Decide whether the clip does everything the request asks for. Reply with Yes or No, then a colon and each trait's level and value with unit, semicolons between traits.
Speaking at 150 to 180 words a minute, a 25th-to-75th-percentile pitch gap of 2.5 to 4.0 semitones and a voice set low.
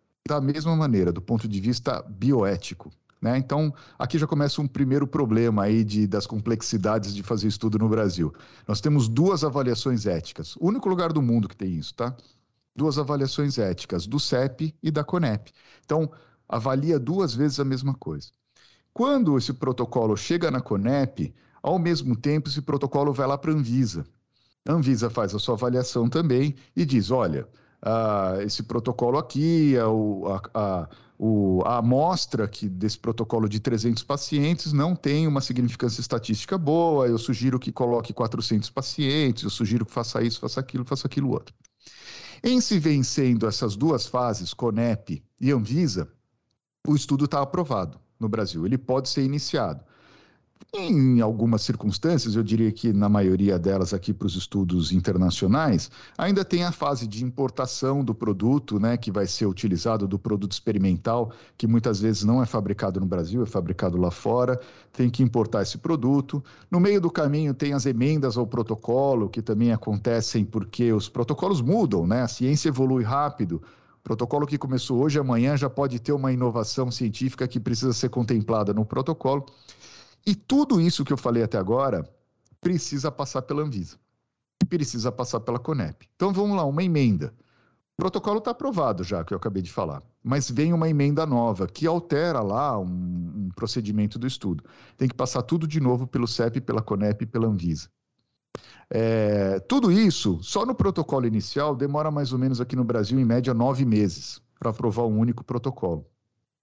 No: average, 170 wpm; average, 4.6 semitones; low, 125 Hz